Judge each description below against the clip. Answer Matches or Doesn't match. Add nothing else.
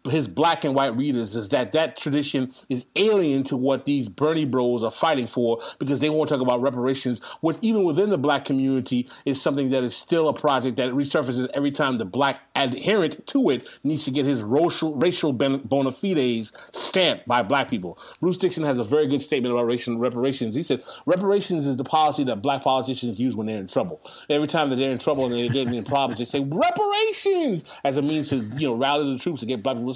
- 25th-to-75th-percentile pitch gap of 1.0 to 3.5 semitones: Matches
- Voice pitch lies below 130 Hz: Doesn't match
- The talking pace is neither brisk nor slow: Doesn't match